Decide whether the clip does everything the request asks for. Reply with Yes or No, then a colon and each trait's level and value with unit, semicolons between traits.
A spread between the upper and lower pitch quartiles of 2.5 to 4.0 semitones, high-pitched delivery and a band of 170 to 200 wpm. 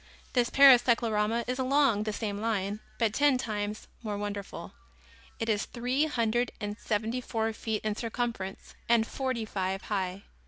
No: average, 2.8 semitones; high, 225 Hz; average, 155 wpm